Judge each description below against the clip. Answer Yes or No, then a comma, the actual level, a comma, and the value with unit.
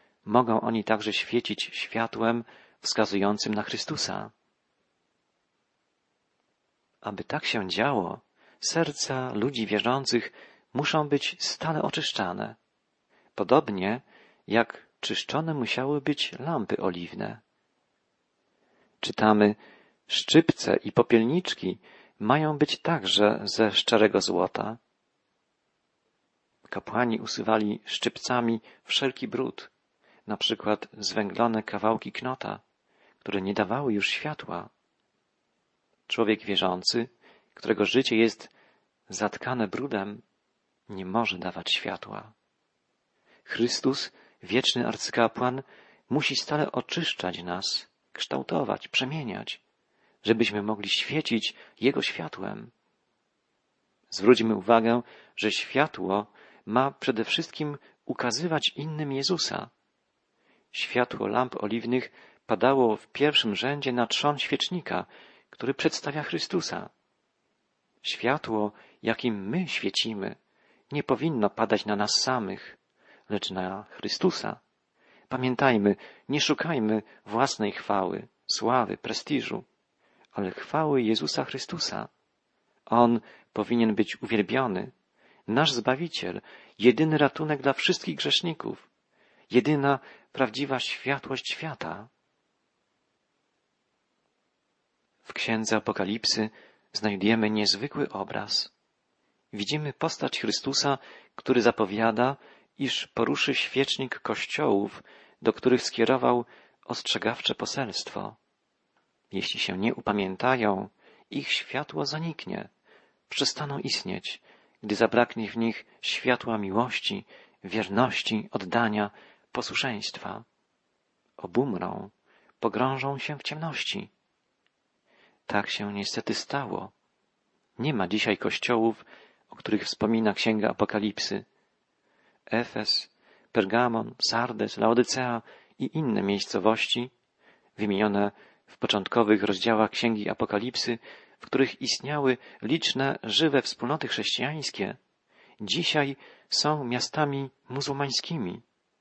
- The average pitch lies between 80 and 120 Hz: Yes, low, 115 Hz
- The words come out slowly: Yes, slow, 90 wpm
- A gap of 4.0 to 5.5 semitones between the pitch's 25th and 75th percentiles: Yes, average, 4.3 semitones